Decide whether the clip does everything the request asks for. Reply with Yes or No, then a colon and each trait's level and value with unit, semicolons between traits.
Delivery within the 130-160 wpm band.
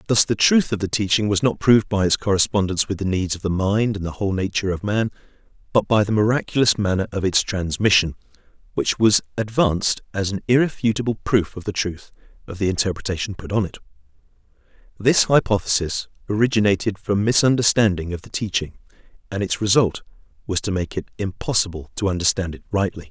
No: average, 175 wpm